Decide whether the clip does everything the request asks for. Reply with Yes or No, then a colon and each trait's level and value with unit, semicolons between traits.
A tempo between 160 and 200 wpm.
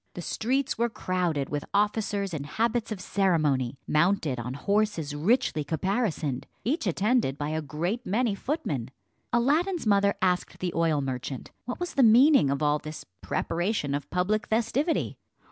No: average, 150 wpm